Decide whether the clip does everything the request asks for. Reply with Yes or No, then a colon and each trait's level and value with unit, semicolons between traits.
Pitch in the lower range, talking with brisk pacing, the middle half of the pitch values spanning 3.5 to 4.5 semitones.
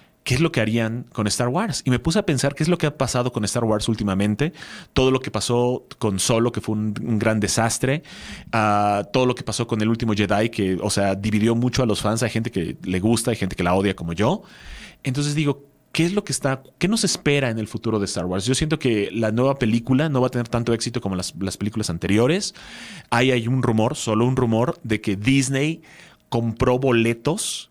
Yes: low, 120 Hz; fast, 235 wpm; average, 3.9 semitones